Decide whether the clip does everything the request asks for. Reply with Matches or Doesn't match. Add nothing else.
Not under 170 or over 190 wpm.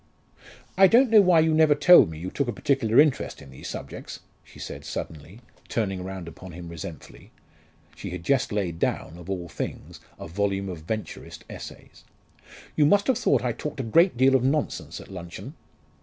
Matches